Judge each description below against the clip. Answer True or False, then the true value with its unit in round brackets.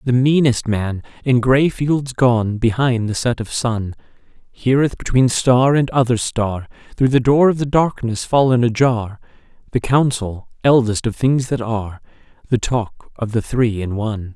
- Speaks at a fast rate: False (165 wpm)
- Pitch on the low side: True (120 Hz)